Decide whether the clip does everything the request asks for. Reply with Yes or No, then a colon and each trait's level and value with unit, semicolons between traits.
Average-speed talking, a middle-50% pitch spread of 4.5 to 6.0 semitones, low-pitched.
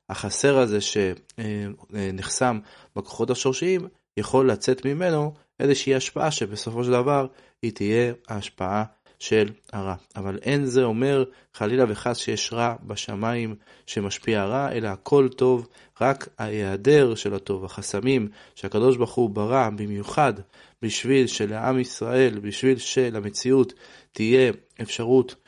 No: average, 115 wpm; average, 3.9 semitones; low, 120 Hz